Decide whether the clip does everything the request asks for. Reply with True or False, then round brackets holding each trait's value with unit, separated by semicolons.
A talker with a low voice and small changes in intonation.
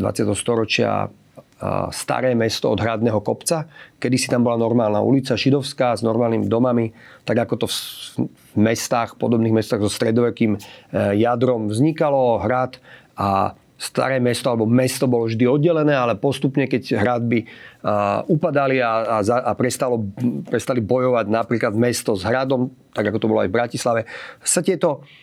True (120 Hz; 2.3 semitones)